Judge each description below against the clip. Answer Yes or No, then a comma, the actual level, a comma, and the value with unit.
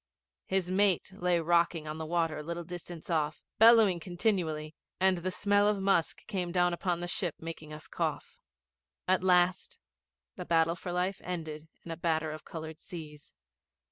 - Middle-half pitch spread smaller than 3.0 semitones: Yes, narrow, 2.6 semitones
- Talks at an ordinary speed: Yes, average, 170 wpm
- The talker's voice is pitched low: No, medium, 175 Hz